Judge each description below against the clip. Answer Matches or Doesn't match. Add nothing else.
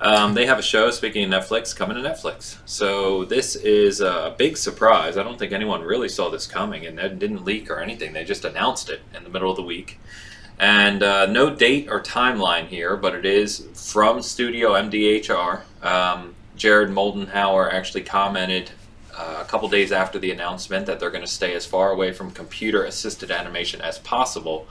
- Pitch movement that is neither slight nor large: Doesn't match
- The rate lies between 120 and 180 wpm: Doesn't match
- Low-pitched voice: Matches